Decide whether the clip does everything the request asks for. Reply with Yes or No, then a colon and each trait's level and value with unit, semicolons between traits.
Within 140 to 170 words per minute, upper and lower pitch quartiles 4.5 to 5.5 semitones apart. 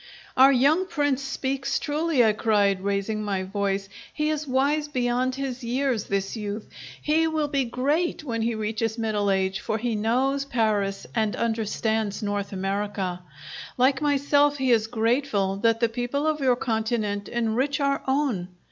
Yes: average, 155 wpm; average, 4.9 semitones